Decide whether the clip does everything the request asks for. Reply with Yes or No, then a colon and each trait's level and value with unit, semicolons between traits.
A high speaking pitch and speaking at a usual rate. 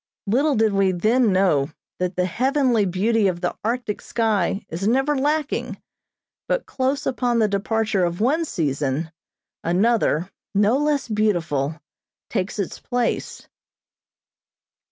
No: high, 210 Hz; slow, 125 wpm